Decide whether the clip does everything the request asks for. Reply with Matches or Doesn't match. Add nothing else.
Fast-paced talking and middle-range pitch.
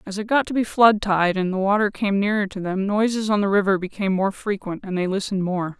Doesn't match